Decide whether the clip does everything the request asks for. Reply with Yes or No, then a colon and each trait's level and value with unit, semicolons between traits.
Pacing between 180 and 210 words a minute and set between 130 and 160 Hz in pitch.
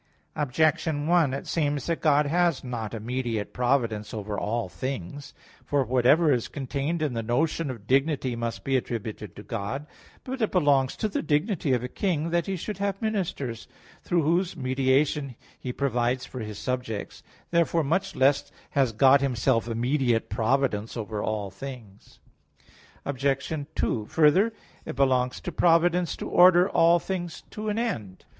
No: average, 155 wpm; low, 135 Hz